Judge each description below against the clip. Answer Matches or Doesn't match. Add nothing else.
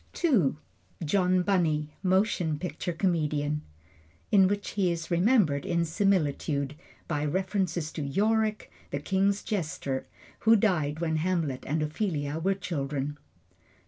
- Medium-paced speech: Doesn't match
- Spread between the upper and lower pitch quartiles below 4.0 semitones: Doesn't match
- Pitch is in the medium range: Matches